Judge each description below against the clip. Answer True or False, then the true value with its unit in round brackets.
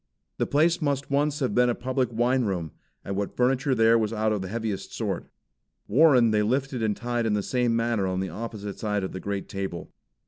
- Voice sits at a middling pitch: False (115 Hz)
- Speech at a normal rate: False (210 wpm)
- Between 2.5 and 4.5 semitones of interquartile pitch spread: True (4.0 semitones)